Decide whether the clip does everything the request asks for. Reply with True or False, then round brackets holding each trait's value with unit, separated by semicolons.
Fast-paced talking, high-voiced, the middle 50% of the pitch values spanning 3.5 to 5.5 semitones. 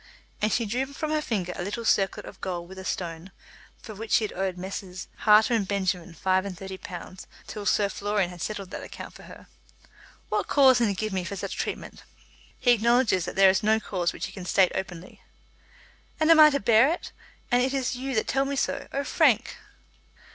True (210 wpm; 205 Hz; 4.6 semitones)